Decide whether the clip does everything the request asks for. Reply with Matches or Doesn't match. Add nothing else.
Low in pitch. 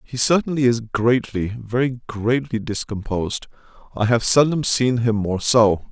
Matches